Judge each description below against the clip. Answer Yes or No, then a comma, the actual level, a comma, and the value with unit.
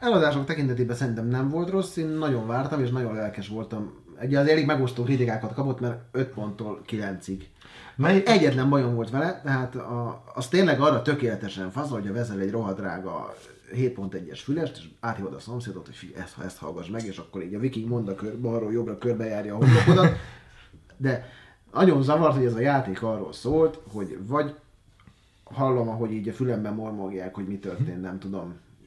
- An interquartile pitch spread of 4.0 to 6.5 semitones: Yes, average, 5.0 semitones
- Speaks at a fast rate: Yes, fast, 180 wpm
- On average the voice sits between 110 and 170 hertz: Yes, low, 120 Hz